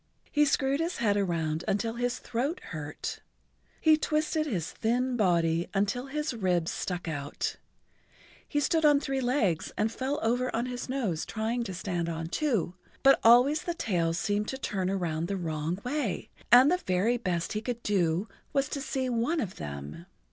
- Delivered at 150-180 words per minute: Yes, average, 175 wpm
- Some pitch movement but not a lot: No, wide, 7.4 semitones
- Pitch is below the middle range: No, high, 225 Hz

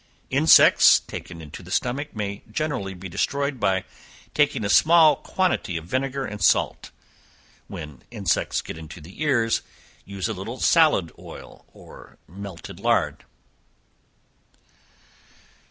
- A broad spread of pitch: Yes, wide, 7.1 semitones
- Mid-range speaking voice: No, low, 105 Hz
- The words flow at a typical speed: No, slow, 120 wpm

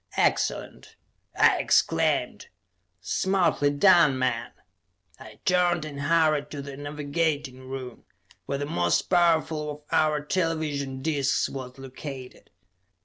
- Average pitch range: Yes, average, 3.0 semitones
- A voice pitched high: No, medium, 145 Hz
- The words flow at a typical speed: No, slow, 110 wpm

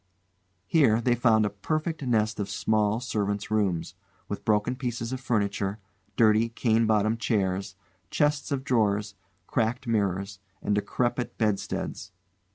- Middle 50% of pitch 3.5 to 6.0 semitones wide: No, average, 2.9 semitones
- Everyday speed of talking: No, slow, 130 wpm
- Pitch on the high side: No, low, 110 Hz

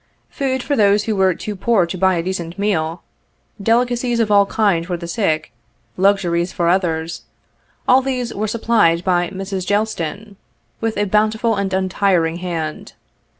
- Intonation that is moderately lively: Yes, average, 3.9 semitones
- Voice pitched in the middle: No, high, 195 Hz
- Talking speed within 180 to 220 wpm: No, average, 160 wpm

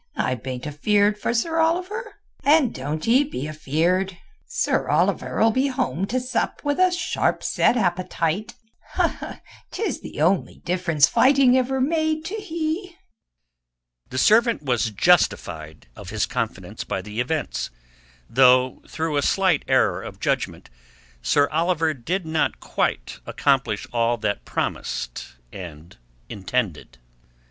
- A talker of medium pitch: Yes, medium, 175 Hz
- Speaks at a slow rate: Yes, slow, 125 wpm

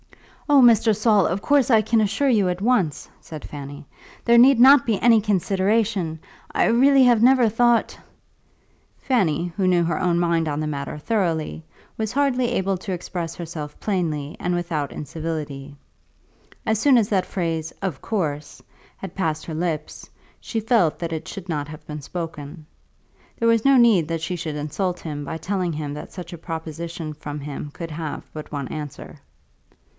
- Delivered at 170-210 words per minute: Yes, average, 175 wpm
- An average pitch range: No, wide, 6.1 semitones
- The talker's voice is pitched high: No, medium, 175 Hz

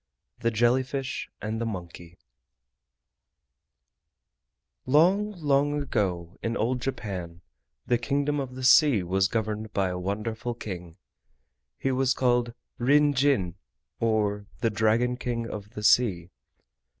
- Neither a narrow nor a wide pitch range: Yes, average, 4.5 semitones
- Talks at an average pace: No, slow, 125 wpm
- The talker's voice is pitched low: Yes, low, 115 Hz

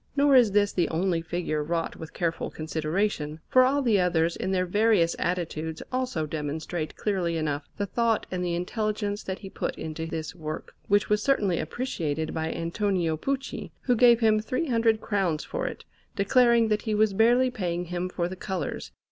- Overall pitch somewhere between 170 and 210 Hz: Yes, medium, 185 Hz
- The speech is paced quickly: No, average, 180 wpm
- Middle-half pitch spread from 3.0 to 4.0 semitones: No, average, 5.0 semitones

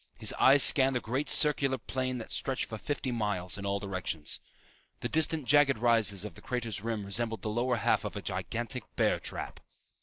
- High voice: No, low, 120 Hz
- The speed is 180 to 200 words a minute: Yes, average, 190 wpm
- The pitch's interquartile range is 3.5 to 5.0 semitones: Yes, average, 3.8 semitones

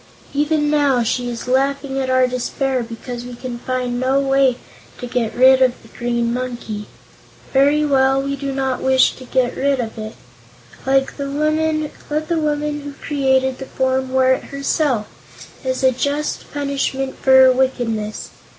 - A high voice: Yes, very high, 265 Hz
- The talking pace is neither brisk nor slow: Yes, average, 160 wpm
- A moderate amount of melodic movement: No, narrow, 1.9 semitones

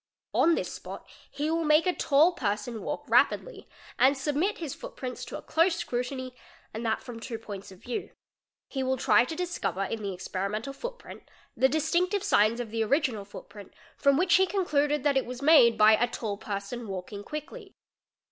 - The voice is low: No, very high, 260 Hz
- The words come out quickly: No, average, 185 wpm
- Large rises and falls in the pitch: Yes, wide, 6.3 semitones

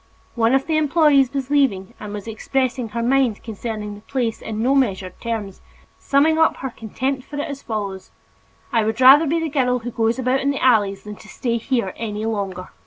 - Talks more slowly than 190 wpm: No, fast, 205 wpm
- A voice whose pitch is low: No, high, 235 Hz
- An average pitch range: Yes, average, 4.2 semitones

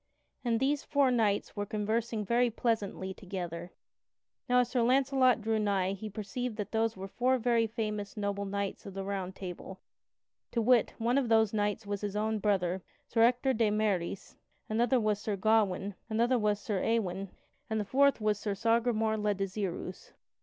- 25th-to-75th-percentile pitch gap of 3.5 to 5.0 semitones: No, average, 2.7 semitones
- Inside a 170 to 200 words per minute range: Yes, average, 175 wpm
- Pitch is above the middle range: Yes, high, 215 Hz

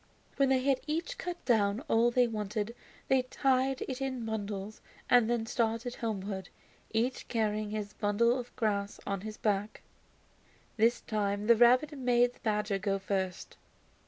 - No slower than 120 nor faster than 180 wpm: Yes, average, 155 wpm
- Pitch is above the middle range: Yes, high, 225 Hz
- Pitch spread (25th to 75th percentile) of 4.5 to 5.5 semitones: No, average, 3.3 semitones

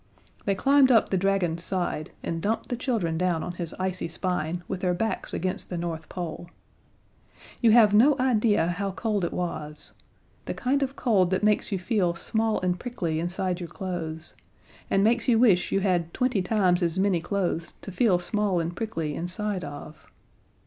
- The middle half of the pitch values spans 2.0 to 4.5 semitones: Yes, average, 3.7 semitones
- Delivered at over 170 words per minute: Yes, average, 180 wpm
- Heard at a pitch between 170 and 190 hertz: Yes, medium, 185 Hz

